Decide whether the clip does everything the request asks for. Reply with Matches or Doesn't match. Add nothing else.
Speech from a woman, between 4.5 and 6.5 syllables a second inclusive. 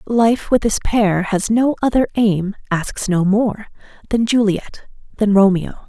Doesn't match